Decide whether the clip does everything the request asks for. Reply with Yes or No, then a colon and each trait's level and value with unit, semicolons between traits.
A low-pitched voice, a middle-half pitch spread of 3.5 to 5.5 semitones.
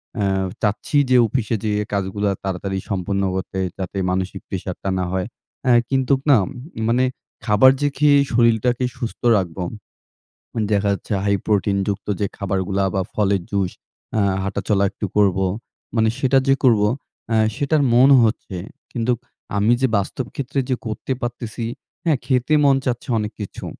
Yes: low, 105 Hz; average, 4.1 semitones